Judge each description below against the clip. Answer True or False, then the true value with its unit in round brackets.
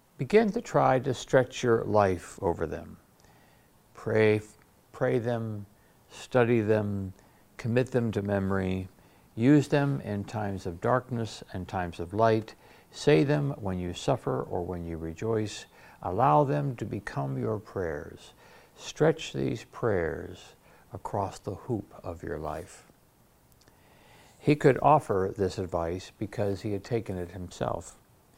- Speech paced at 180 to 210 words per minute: False (135 wpm)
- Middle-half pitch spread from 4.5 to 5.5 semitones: True (5.0 semitones)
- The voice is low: True (105 Hz)